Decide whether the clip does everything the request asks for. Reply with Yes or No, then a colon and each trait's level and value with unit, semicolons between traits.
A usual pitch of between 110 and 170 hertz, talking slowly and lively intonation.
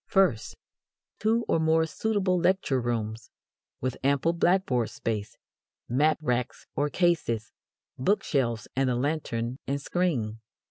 Yes: medium, 140 Hz; slow, 125 wpm; wide, 6.6 semitones